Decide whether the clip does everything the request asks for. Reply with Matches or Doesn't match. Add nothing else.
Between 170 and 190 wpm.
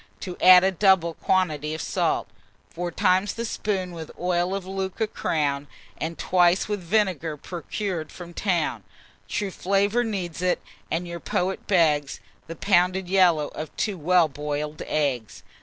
Doesn't match